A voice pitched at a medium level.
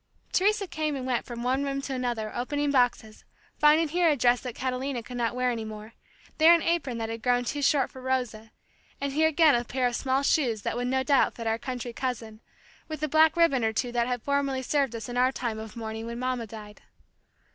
No: very high, 250 Hz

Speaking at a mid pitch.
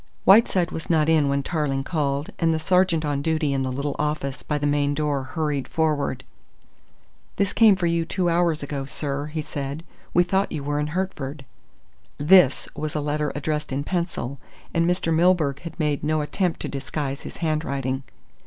Yes: medium, 150 Hz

